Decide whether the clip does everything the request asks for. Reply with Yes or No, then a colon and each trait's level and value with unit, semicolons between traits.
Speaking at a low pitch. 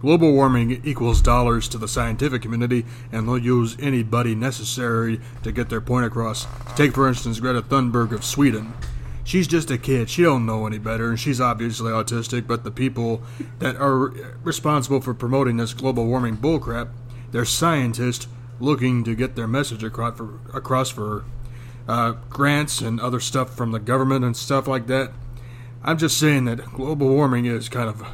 Yes: low, 120 Hz